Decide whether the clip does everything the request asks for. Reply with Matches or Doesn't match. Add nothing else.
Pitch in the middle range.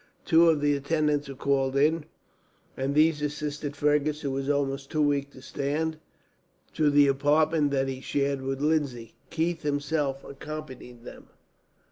Matches